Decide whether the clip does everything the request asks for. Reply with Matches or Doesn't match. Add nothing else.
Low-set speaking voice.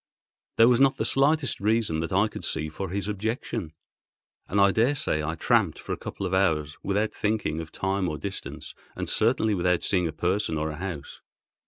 Matches